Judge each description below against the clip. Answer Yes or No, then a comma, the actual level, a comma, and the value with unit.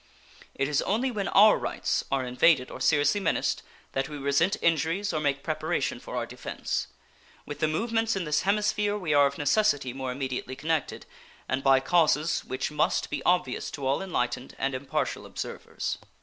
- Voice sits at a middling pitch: Yes, medium, 150 Hz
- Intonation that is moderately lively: No, wide, 5.8 semitones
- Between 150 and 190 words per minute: Yes, average, 175 wpm